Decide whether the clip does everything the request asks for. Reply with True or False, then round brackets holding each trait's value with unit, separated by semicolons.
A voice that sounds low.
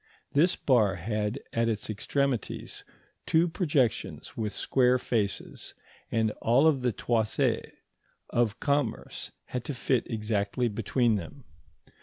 True (120 Hz)